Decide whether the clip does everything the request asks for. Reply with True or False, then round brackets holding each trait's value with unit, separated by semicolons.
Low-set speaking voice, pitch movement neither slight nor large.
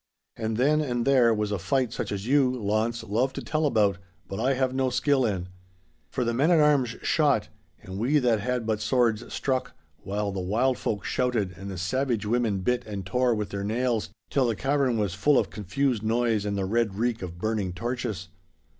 True (115 Hz; 3.8 semitones)